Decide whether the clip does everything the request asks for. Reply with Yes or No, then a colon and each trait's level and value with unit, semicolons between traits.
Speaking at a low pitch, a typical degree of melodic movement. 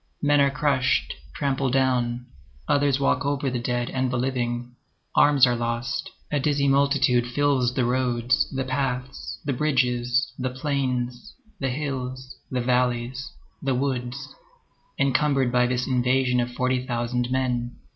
No: low, 130 Hz; narrow, 1.9 semitones